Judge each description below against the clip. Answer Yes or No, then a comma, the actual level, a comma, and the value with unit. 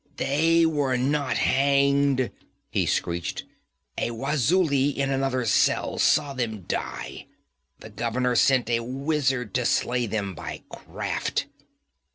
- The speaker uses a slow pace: Yes, slow, 120 wpm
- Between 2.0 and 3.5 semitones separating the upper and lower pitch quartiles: Yes, average, 2.9 semitones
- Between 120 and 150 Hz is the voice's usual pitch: Yes, low, 135 Hz